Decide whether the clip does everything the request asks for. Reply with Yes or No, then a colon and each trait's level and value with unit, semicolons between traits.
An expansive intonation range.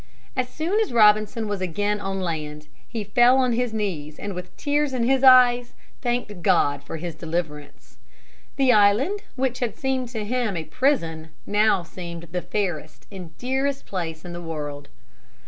Yes: wide, 6.8 semitones